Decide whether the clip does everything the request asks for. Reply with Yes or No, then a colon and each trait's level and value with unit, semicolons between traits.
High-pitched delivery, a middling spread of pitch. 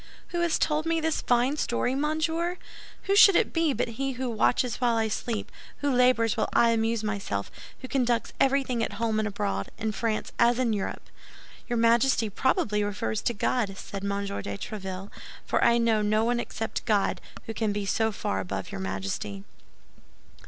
Yes: high, 230 Hz; average, 3.9 semitones